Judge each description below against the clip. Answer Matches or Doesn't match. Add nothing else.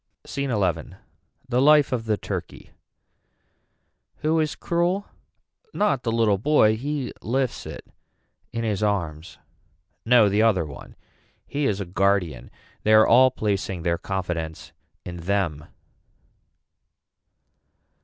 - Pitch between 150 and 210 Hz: Doesn't match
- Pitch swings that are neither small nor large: Doesn't match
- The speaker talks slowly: Matches